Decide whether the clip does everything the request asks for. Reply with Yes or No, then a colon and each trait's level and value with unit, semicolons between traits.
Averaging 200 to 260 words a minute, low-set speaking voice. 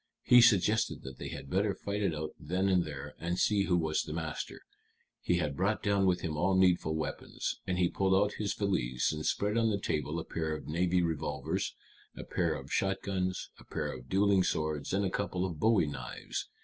Yes: fast, 205 wpm; very low, 90 Hz